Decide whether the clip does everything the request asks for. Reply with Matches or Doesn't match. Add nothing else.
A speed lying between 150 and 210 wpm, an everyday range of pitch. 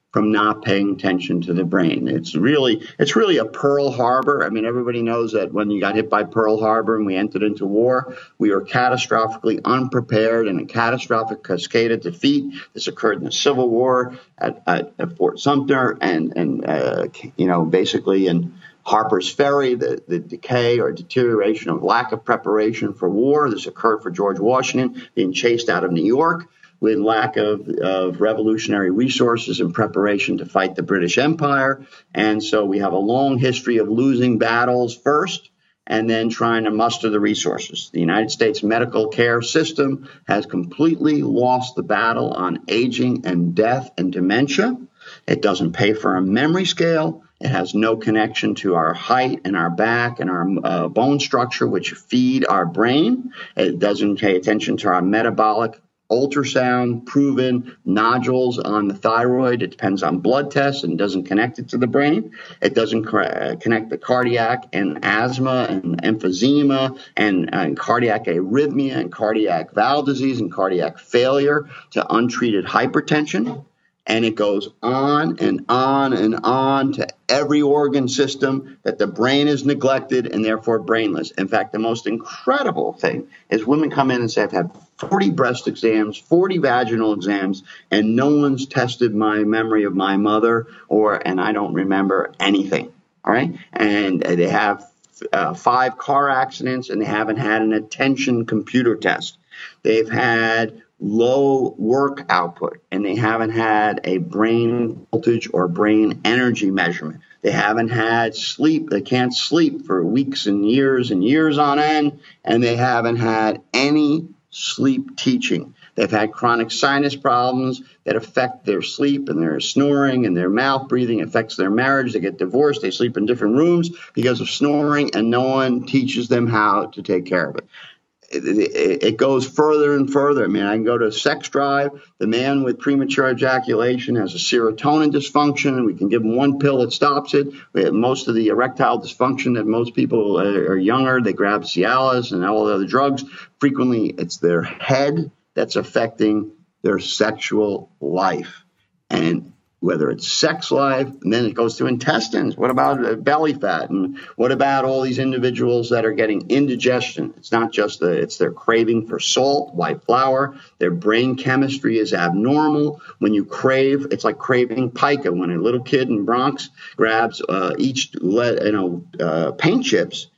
Matches